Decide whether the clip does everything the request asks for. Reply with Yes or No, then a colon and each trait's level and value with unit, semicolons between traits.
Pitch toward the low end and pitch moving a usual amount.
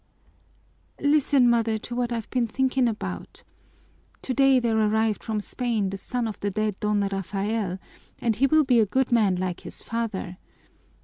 No: high, 225 Hz; average, 3.1 semitones